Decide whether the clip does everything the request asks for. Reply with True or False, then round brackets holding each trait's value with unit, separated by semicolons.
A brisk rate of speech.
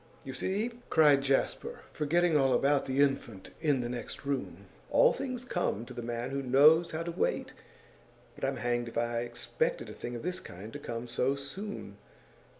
False (185 wpm)